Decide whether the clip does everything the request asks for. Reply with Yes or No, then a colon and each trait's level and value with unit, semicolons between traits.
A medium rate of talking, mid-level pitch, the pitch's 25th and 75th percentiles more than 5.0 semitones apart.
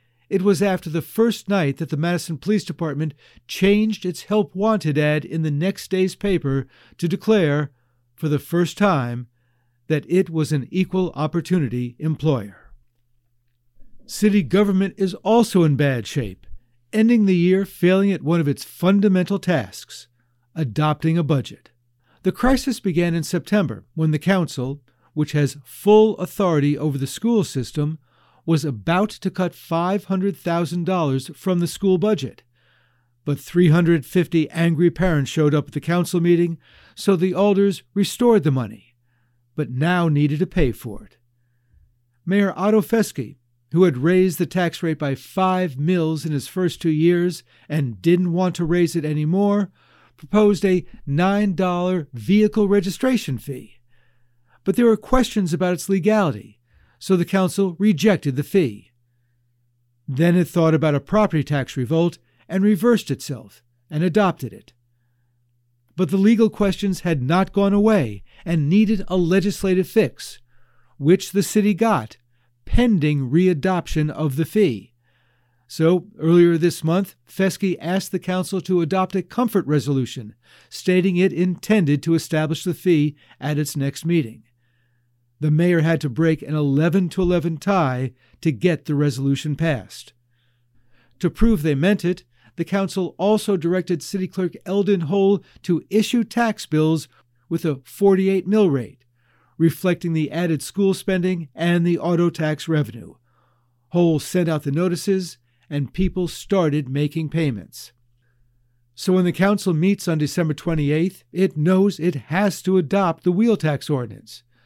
Yes: average, 145 wpm; medium, 165 Hz; wide, 5.5 semitones